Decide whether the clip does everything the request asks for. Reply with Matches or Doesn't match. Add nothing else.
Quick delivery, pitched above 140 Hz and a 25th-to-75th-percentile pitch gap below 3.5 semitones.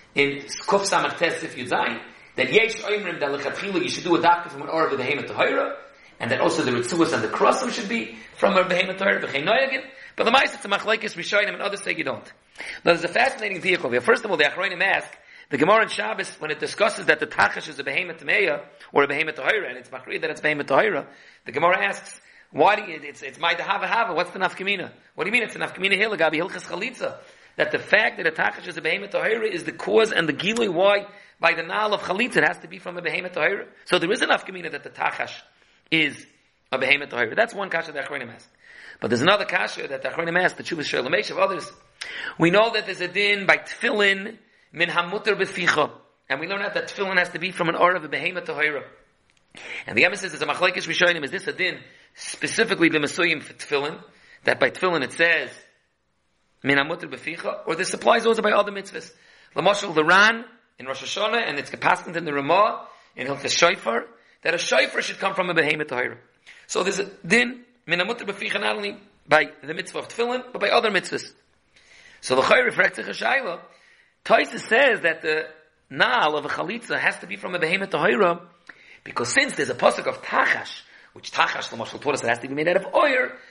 Doesn't match